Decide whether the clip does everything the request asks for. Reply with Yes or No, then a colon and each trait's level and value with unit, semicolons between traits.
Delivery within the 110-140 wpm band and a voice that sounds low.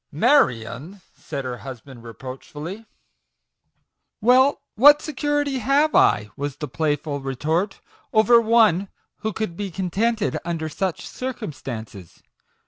No: slow, 135 wpm; medium, 175 Hz